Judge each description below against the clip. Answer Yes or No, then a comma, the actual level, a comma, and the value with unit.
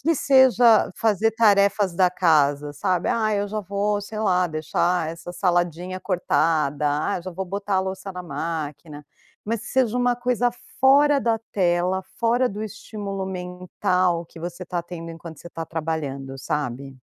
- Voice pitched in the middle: Yes, medium, 180 Hz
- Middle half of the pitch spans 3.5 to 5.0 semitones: Yes, average, 4.1 semitones